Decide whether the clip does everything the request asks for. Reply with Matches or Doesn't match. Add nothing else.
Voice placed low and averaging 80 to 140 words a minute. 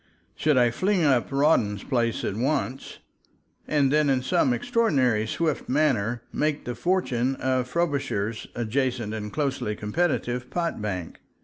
Matches